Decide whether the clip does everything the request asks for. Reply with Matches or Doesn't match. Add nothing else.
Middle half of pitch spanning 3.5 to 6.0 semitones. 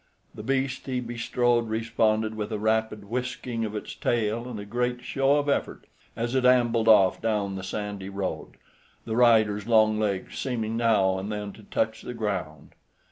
Doesn't match